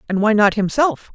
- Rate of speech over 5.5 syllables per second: No, 5.2 syllables/s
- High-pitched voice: Yes, high, 215 Hz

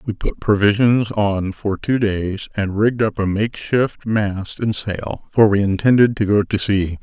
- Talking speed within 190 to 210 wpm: Yes, average, 195 wpm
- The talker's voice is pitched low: Yes, low, 105 Hz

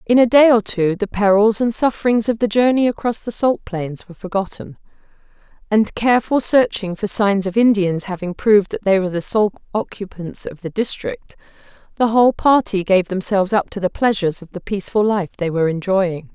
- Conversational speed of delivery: Yes, average, 190 wpm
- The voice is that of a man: No, female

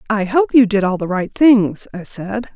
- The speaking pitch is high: Yes, high, 215 Hz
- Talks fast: Yes, fast, 235 wpm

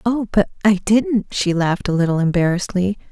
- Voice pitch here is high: Yes, high, 195 Hz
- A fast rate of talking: No, average, 175 wpm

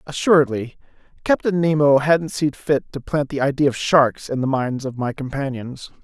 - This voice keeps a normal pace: Yes, average, 180 wpm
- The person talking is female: No, male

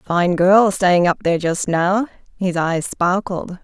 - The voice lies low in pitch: No, medium, 185 Hz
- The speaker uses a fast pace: No, average, 165 wpm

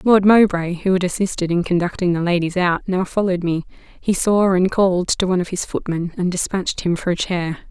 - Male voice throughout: No, female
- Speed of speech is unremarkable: No, fast, 220 wpm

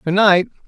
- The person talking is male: Yes, male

